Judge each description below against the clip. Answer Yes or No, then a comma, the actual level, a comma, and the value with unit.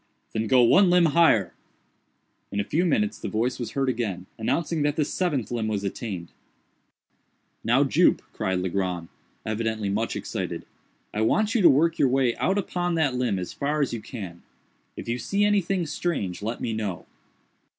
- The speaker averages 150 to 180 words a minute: Yes, average, 175 wpm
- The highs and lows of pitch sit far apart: Yes, wide, 7.7 semitones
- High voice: No, low, 120 Hz